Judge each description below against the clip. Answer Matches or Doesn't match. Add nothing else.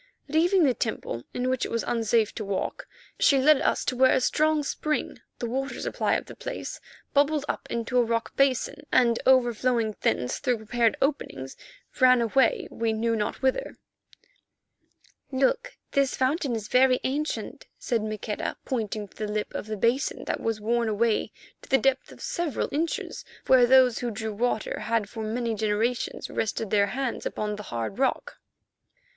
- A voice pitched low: Doesn't match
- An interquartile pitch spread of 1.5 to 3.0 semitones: Doesn't match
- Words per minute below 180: Matches